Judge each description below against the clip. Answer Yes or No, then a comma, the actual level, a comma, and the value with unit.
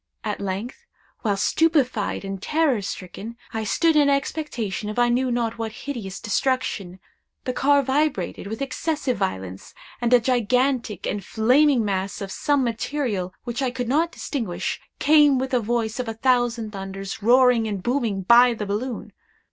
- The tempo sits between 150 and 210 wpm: Yes, average, 160 wpm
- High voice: Yes, high, 240 Hz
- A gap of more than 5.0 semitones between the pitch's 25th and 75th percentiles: No, average, 4.3 semitones